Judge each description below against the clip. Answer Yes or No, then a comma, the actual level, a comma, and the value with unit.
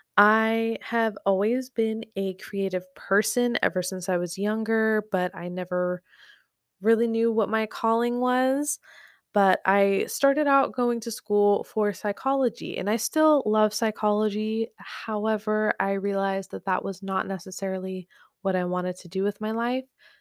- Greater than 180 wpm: No, average, 150 wpm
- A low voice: No, high, 215 Hz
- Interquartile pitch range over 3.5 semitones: No, average, 2.8 semitones